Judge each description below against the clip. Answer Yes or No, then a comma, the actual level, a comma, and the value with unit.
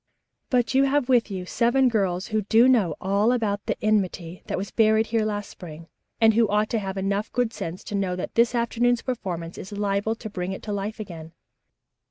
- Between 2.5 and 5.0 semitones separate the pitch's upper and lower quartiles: Yes, average, 3.3 semitones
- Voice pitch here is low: No, high, 210 Hz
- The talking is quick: Yes, fast, 210 wpm